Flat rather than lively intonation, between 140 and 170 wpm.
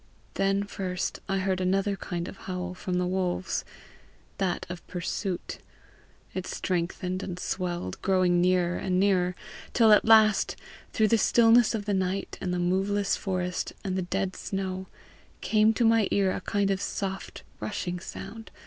Yes: narrow, 1.8 semitones; average, 160 wpm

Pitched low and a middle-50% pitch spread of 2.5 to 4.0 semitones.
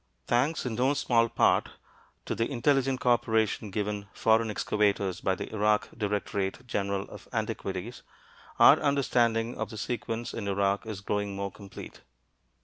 Yes: low, 110 Hz; average, 3.0 semitones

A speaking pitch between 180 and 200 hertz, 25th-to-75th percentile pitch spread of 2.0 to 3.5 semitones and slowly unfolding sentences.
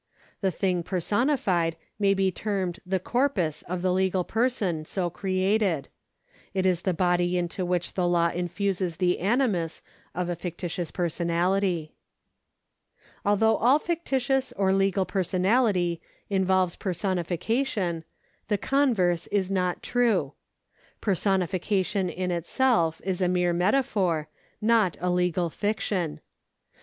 Yes: medium, 185 Hz; average, 2.7 semitones; slow, 120 wpm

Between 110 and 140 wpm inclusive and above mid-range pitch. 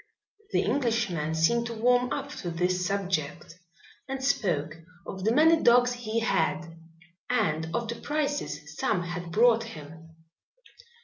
Yes: slow, 135 wpm; high, 200 Hz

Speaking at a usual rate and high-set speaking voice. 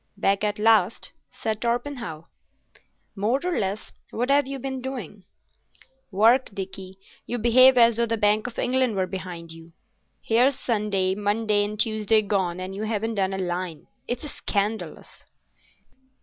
Yes: average, 150 wpm; high, 215 Hz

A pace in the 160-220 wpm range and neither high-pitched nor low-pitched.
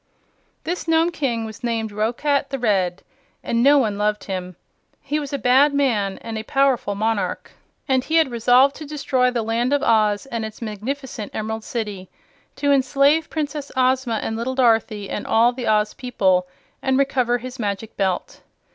No: average, 175 wpm; high, 240 Hz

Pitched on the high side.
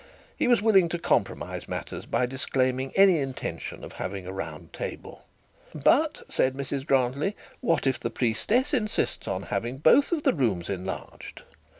No: low, 135 Hz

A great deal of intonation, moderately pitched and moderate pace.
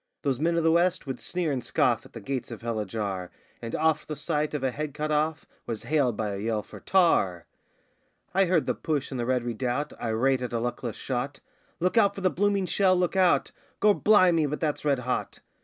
No: wide, 5.8 semitones; medium, 145 Hz; fast, 225 wpm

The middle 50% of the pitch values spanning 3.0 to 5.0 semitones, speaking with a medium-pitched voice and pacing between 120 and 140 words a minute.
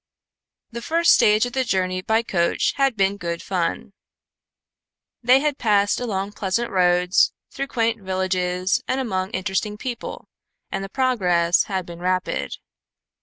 No: average, 4.3 semitones; high, 195 Hz; slow, 135 wpm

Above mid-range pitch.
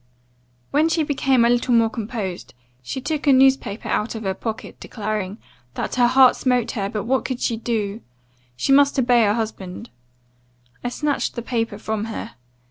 Yes: high, 235 Hz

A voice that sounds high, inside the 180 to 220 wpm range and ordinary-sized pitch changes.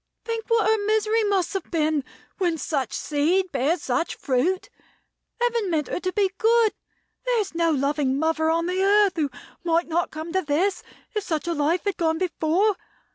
Yes: very high, 345 Hz; average, 185 wpm; average, 4.5 semitones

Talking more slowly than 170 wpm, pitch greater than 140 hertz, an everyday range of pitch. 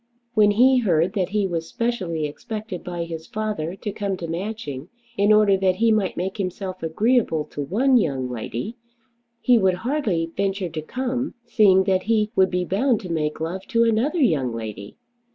No: average, 180 wpm; high, 190 Hz; average, 4.9 semitones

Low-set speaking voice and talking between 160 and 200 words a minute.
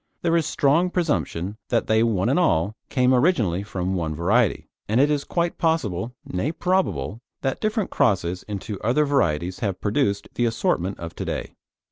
Yes: low, 115 Hz; average, 170 wpm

